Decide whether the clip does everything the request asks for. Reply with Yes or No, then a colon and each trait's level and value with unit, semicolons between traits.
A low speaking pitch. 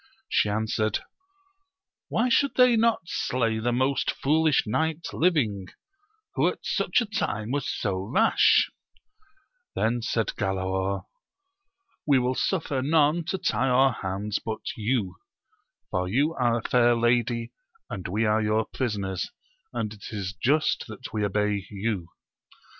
Yes: low, 115 Hz